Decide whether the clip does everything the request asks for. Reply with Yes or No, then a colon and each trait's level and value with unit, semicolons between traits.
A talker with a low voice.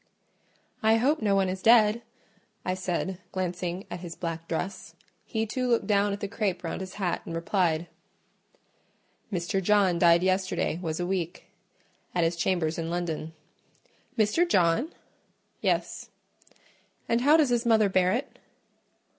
No: medium, 185 Hz